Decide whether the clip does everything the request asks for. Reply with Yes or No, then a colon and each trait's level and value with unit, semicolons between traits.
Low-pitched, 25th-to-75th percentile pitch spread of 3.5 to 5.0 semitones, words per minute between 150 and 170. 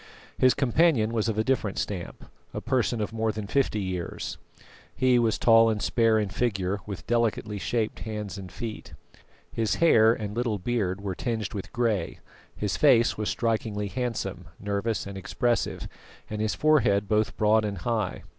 No: low, 110 Hz; average, 2.7 semitones; average, 165 wpm